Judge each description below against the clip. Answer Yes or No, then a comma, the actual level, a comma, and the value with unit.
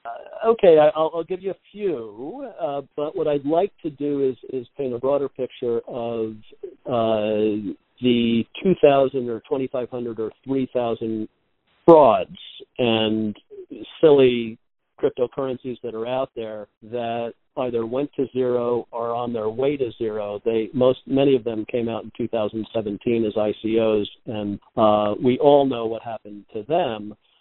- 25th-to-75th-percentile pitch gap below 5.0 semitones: Yes, average, 4.0 semitones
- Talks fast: No, average, 155 wpm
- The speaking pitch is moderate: No, low, 120 Hz